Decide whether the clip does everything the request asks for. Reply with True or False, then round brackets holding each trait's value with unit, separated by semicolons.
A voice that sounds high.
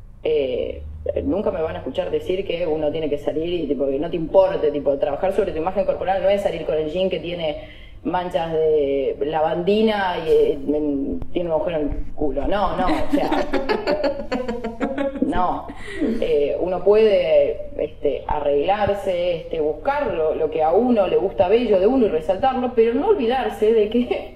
True (195 Hz)